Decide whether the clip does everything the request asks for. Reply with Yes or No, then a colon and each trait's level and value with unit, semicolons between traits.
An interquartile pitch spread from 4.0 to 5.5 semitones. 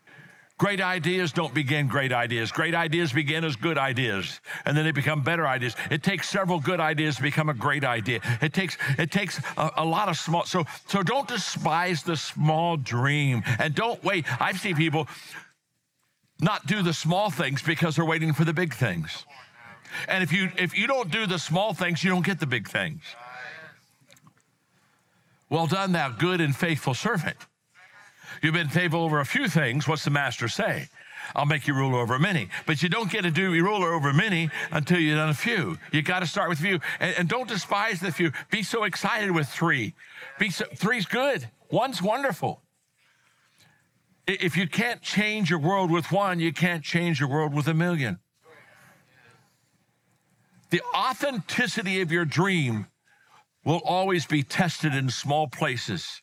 No: average, 3.4 semitones